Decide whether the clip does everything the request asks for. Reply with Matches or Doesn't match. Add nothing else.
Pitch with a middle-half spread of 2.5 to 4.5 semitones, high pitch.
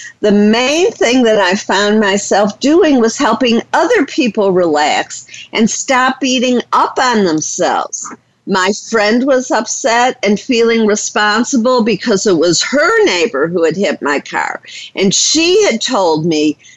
Matches